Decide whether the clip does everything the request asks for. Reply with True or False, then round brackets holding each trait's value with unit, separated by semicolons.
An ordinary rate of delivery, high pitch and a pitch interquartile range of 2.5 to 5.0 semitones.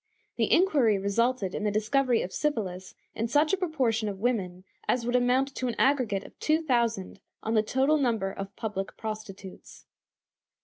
True (170 wpm; 230 Hz; 4.7 semitones)